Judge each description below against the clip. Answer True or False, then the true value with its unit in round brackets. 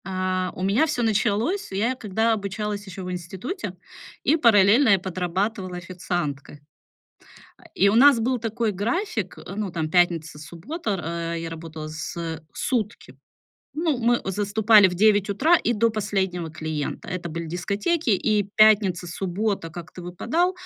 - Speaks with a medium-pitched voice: False (195 Hz)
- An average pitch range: True (4.2 semitones)